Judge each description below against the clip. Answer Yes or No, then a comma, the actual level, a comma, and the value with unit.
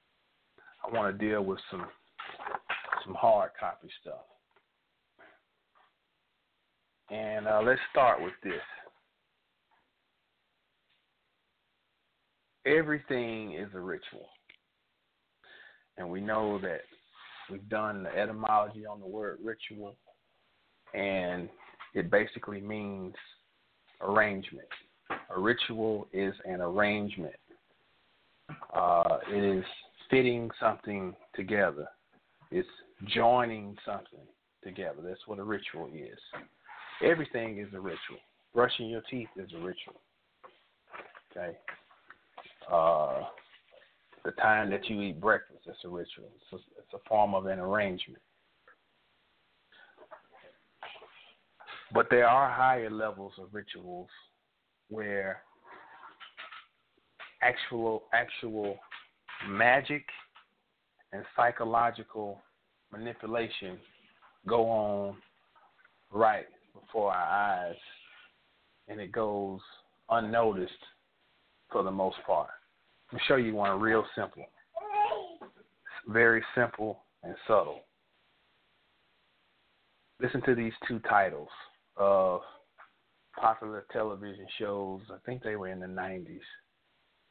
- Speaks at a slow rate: Yes, slow, 95 wpm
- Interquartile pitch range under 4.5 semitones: Yes, narrow, 2.6 semitones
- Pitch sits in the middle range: No, low, 105 Hz